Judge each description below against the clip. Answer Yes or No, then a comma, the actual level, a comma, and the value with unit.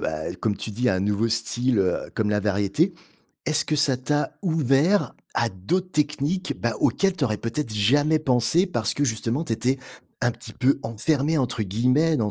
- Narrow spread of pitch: No, wide, 5.6 semitones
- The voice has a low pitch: Yes, low, 125 Hz